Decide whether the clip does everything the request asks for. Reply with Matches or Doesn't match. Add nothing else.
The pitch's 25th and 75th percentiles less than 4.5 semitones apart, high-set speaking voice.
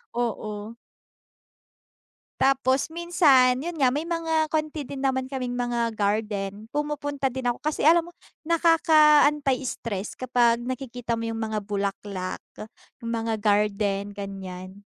Doesn't match